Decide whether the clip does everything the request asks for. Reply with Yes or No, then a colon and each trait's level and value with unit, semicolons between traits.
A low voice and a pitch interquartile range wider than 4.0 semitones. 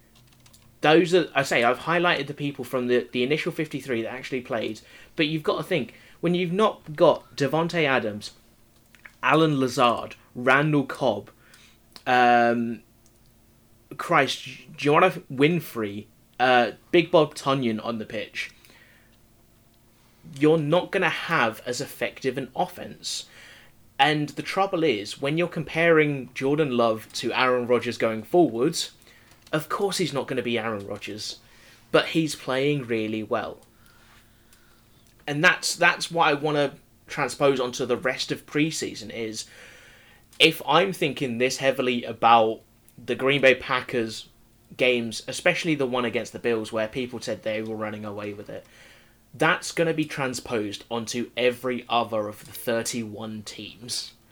Yes: low, 125 Hz; average, 4.5 semitones